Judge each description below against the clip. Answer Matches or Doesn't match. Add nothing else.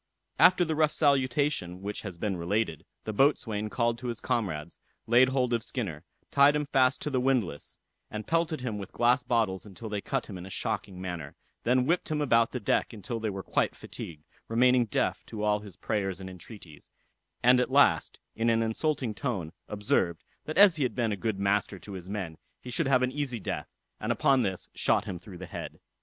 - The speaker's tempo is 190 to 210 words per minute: Matches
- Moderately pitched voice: Doesn't match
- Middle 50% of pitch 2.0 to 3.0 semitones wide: Doesn't match